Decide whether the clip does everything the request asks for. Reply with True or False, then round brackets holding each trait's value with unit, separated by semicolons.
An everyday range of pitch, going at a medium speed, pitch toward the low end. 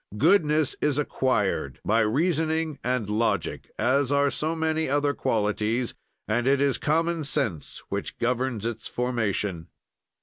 False (5.0 semitones; 130 wpm; 130 Hz)